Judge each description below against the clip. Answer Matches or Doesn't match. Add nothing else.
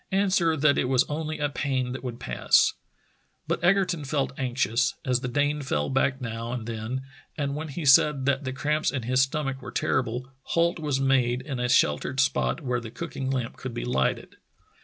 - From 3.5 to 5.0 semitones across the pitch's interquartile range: Doesn't match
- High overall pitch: Doesn't match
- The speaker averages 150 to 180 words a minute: Doesn't match